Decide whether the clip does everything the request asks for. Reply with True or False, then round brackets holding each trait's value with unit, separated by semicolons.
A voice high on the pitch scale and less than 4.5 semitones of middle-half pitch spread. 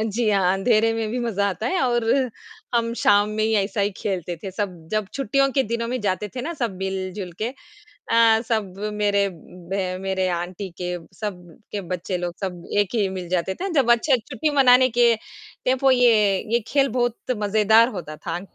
True (210 Hz; 3.9 semitones)